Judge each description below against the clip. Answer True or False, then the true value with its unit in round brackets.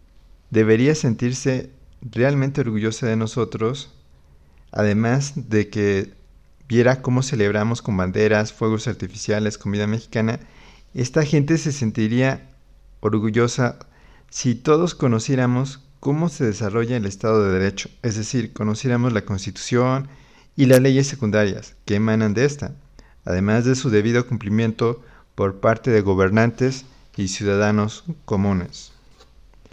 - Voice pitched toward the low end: True (110 Hz)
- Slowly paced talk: True (115 wpm)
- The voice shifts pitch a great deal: False (3.7 semitones)